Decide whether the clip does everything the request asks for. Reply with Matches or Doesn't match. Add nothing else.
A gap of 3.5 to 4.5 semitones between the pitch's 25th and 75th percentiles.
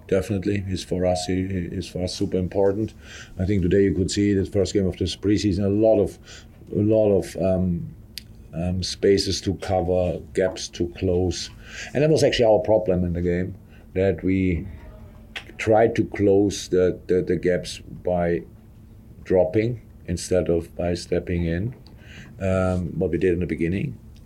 Doesn't match